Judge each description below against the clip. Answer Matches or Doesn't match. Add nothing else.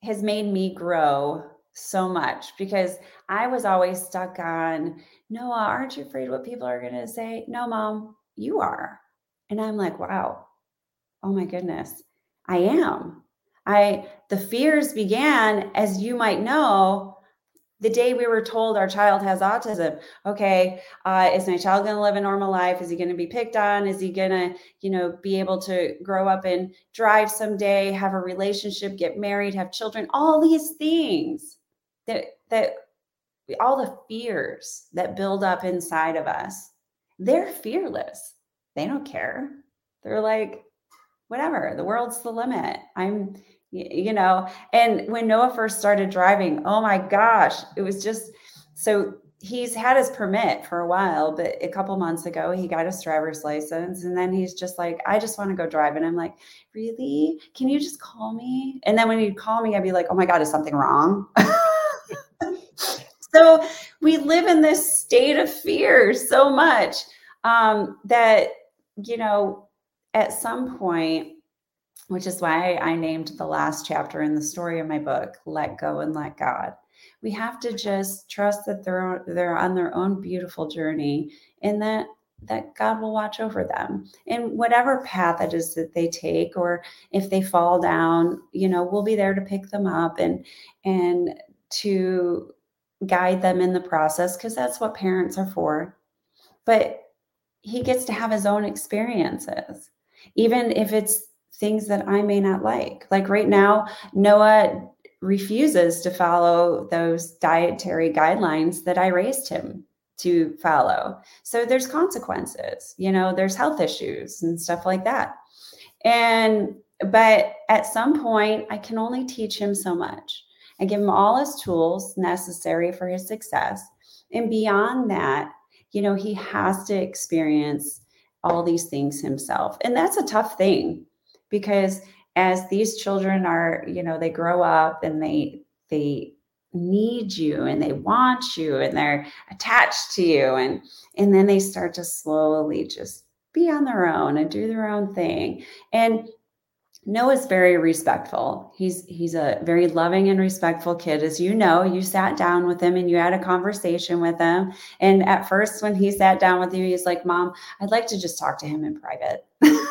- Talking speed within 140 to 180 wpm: Matches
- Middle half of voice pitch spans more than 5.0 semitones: Doesn't match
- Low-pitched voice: Doesn't match